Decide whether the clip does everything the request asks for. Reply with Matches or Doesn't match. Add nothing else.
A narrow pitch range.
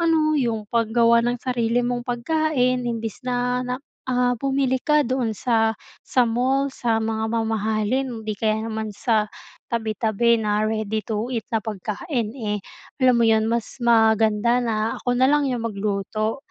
Matches